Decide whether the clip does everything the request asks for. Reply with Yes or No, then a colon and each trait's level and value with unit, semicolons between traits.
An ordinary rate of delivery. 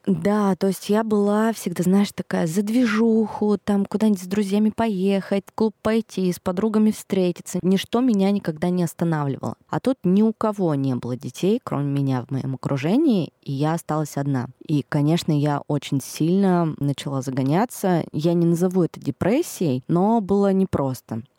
No: fast, 165 wpm